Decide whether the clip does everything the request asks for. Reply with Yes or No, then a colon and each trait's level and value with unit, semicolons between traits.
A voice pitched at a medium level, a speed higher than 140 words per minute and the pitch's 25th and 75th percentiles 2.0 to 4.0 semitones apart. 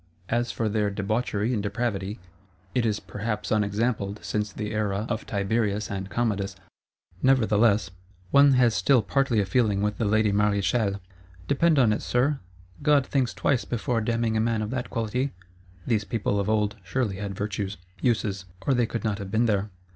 No: low, 110 Hz; average, 170 wpm; average, 2.9 semitones